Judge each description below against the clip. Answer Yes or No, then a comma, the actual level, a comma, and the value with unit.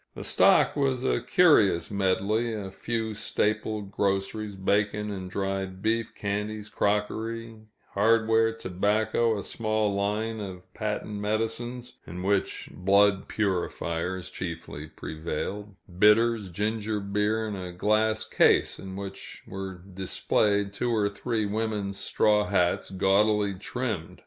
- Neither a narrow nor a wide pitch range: No, narrow, 2.2 semitones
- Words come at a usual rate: No, slow, 120 wpm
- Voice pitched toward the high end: No, low, 105 Hz